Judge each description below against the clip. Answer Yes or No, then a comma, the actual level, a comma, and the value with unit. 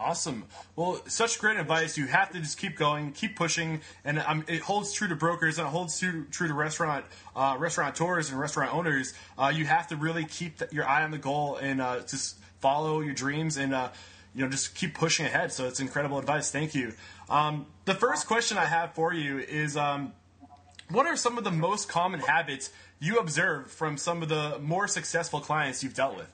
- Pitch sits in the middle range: Yes, medium, 155 Hz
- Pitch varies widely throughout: No, average, 3.7 semitones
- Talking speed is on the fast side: Yes, fast, 215 wpm